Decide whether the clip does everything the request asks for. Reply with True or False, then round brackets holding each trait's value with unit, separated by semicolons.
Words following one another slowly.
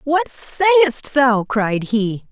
True (130 wpm)